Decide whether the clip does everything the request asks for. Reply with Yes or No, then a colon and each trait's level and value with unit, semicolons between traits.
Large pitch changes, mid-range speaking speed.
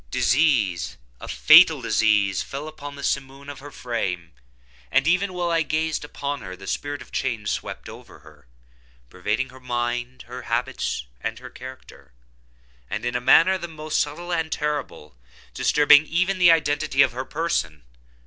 No: average, 4.9 semitones; average, 160 wpm